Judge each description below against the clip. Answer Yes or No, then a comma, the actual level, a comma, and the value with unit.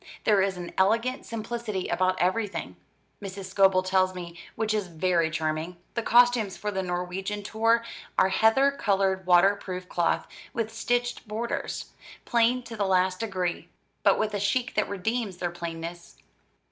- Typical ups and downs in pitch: Yes, average, 3.6 semitones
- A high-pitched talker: Yes, high, 195 Hz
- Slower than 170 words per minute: Yes, average, 155 wpm